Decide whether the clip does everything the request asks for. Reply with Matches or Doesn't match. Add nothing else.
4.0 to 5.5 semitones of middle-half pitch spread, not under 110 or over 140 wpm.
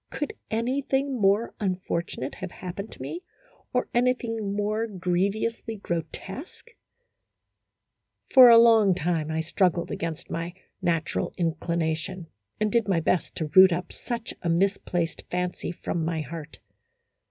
Matches